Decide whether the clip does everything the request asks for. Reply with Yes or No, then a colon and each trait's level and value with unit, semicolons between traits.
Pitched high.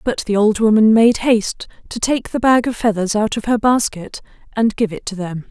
Yes: high, 220 Hz